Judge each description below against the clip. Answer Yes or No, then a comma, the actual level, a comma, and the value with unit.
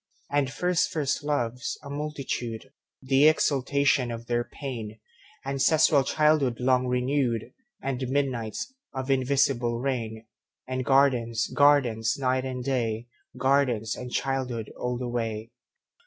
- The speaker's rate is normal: No, slow, 100 wpm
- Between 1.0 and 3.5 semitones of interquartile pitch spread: Yes, average, 2.9 semitones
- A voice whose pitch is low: Yes, low, 130 Hz